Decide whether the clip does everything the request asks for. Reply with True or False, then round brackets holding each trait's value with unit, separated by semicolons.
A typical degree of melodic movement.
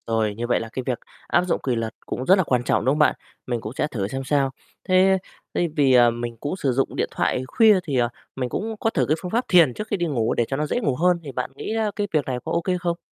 False (6.6 semitones)